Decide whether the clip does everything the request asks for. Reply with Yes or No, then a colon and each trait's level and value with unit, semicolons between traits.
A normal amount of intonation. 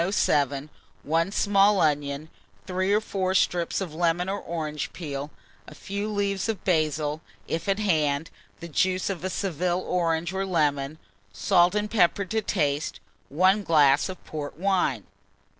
Yes: average, 4.2 semitones